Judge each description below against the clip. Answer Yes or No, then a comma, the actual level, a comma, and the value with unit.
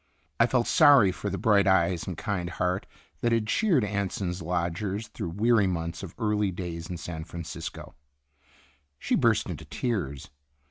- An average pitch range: Yes, average, 3.8 semitones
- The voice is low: Yes, very low, 95 Hz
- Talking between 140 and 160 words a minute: Yes, average, 155 wpm